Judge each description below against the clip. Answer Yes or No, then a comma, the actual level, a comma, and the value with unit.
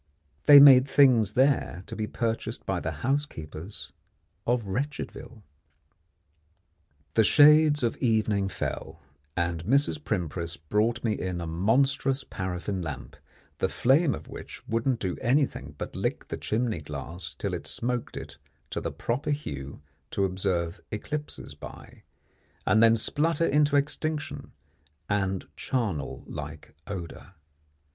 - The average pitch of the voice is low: Yes, low, 110 Hz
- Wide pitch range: Yes, wide, 7.2 semitones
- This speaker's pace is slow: Yes, slow, 130 wpm